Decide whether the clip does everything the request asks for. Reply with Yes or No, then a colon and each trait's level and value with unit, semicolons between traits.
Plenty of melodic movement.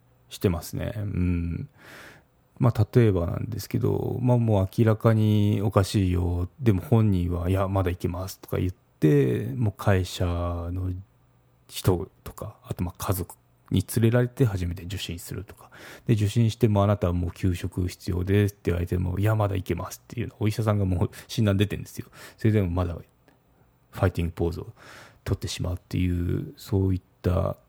No: average, 4.2 semitones